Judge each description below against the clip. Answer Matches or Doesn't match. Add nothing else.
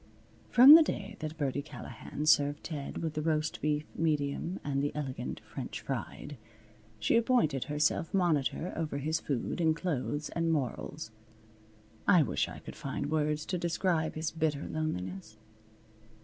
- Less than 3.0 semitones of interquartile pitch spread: Matches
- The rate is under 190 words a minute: Matches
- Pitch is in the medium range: Matches